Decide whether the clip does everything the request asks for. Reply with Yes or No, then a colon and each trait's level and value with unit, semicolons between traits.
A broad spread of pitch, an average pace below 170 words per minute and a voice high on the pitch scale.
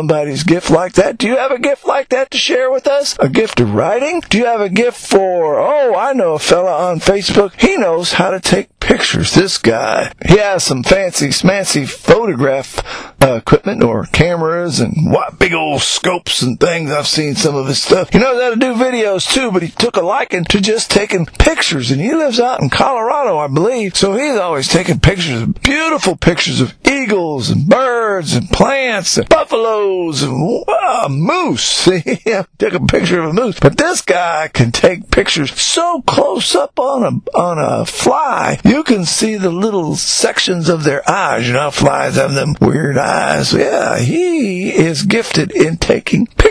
No: wide, 6.7 semitones; average, 195 wpm; high, 195 Hz